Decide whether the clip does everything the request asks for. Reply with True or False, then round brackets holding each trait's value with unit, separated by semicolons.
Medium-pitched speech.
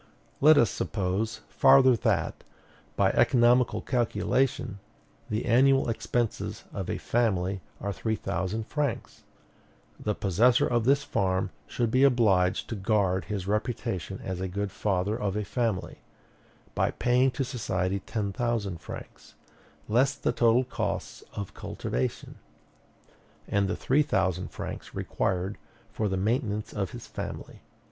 False (110 Hz)